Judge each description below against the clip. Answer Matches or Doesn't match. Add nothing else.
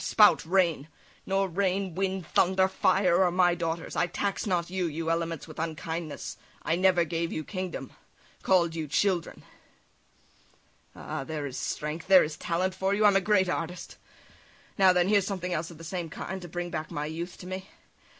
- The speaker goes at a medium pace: Matches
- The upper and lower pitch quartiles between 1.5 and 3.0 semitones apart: Matches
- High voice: Doesn't match